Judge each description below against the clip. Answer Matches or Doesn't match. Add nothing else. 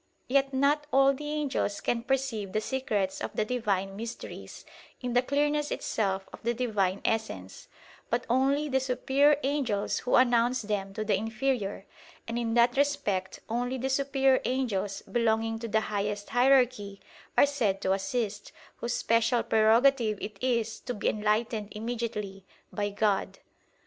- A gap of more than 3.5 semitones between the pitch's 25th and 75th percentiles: Matches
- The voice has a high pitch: Matches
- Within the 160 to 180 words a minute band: Doesn't match